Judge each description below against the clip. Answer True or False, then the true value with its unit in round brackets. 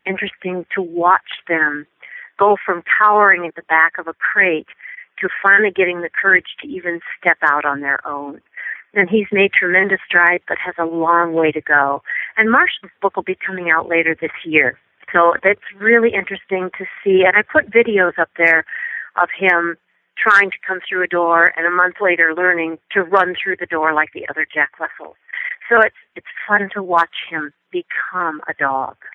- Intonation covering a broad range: False (2.8 semitones)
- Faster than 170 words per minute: True (190 wpm)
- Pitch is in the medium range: True (180 Hz)